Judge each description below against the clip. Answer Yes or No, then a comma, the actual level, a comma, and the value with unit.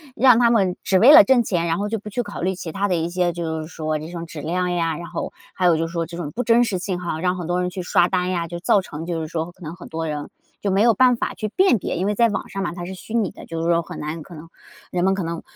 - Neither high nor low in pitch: Yes, medium, 180 Hz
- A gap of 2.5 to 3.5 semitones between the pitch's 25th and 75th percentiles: Yes, average, 3.1 semitones